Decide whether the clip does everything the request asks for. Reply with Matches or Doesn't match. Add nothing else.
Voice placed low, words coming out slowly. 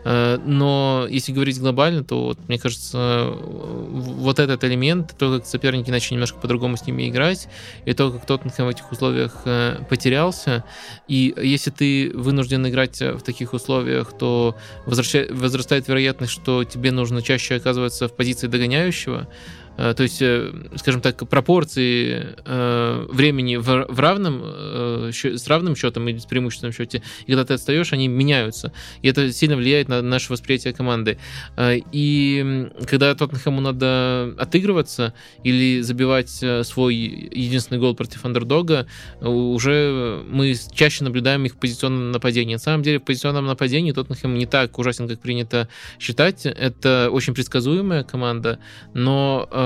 Doesn't match